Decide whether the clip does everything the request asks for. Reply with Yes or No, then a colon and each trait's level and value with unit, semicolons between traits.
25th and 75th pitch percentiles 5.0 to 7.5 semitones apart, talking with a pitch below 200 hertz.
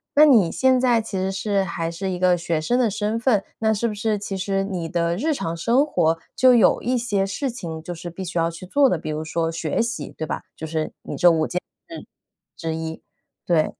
Yes: wide, 5.6 semitones; high, 190 Hz